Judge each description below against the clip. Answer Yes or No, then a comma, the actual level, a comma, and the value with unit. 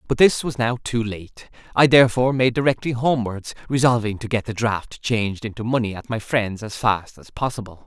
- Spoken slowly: No, average, 200 wpm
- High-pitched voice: No, low, 115 Hz